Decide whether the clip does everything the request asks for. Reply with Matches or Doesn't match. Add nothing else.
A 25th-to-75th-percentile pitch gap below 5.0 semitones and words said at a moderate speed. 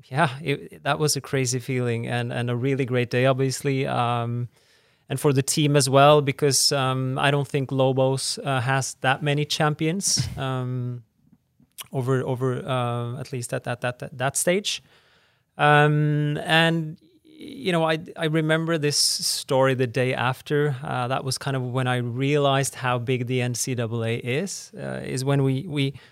Matches